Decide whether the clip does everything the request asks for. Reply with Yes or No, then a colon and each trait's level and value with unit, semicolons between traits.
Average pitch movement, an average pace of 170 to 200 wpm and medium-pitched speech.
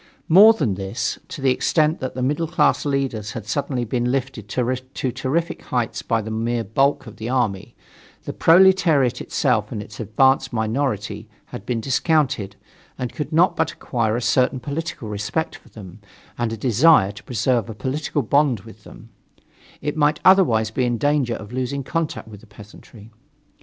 No: average, 4.7 semitones; average, 175 wpm; low, 125 Hz